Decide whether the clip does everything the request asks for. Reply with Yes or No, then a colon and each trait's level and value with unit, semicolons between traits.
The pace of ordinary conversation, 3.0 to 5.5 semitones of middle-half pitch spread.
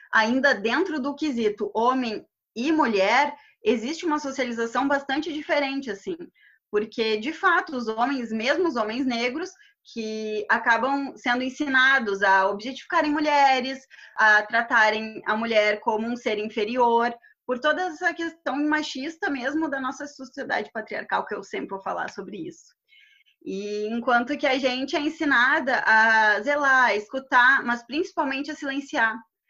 Yes: average, 140 wpm; average, 5.1 semitones